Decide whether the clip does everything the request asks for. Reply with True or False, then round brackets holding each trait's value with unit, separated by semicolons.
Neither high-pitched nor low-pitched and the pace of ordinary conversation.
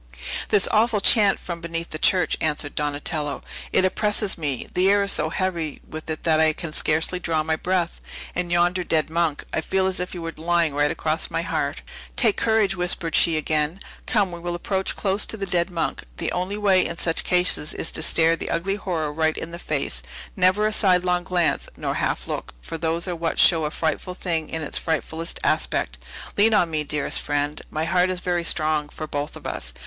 False (170 Hz; 210 wpm)